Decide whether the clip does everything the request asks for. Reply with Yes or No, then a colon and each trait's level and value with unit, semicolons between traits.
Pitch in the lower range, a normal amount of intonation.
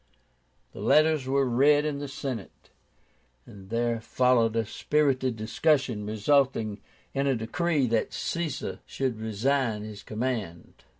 Yes: low, 125 Hz; average, 4.2 semitones